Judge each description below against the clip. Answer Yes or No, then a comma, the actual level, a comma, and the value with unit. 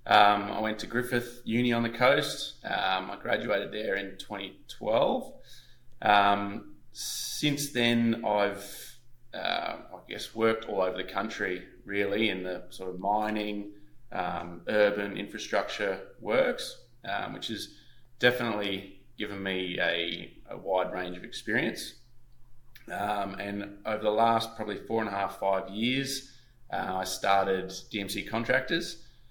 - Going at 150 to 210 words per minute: No, slow, 135 wpm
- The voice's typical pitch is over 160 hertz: No, low, 105 Hz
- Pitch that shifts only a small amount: No, average, 3.5 semitones